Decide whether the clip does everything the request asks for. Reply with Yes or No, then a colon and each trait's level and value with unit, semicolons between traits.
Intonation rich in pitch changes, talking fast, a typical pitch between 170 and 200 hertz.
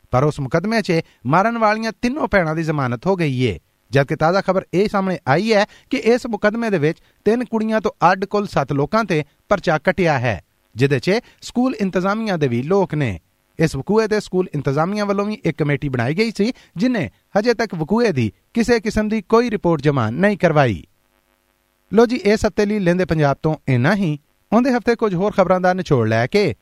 Yes: wide, 6.7 semitones; fast, 200 wpm; medium, 185 Hz